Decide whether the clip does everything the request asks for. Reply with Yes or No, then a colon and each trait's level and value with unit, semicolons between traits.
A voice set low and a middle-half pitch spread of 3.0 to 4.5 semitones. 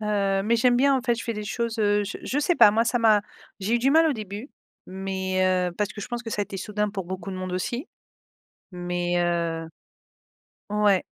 No: high, 210 Hz; average, 3.8 semitones